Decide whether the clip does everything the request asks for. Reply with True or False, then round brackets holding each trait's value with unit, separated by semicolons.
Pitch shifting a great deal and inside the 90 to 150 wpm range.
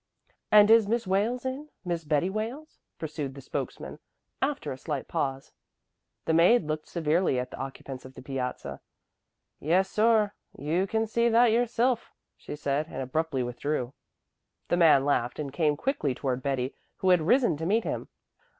False (8.1 semitones; 165 wpm)